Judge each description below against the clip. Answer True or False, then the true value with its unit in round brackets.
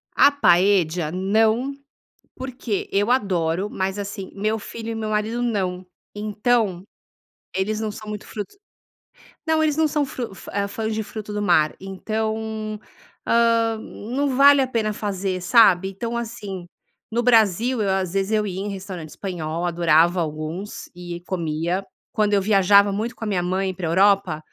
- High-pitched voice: True (205 Hz)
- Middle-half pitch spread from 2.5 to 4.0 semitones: True (3.2 semitones)